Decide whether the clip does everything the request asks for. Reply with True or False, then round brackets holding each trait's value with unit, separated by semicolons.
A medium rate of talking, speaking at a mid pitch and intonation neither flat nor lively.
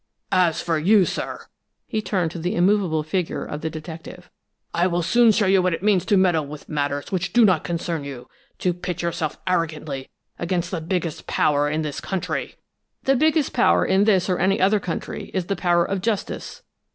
True (195 wpm; 175 Hz; 3.2 semitones)